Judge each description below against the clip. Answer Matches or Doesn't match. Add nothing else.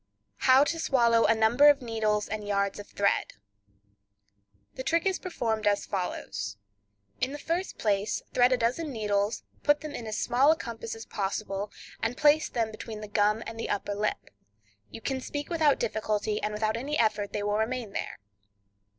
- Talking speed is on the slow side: Doesn't match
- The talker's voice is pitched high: Matches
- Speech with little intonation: Doesn't match